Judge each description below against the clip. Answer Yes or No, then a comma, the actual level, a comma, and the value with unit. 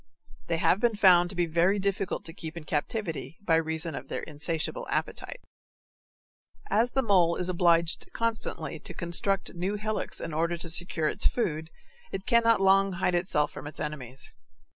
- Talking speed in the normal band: Yes, average, 170 wpm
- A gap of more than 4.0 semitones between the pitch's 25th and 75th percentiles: No, average, 3.5 semitones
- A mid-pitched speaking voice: Yes, medium, 175 Hz